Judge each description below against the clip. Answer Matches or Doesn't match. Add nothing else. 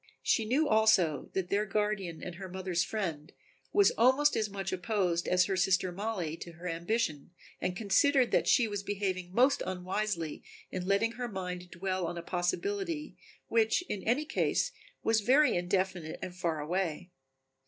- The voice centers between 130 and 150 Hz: Doesn't match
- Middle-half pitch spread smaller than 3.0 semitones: Doesn't match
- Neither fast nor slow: Matches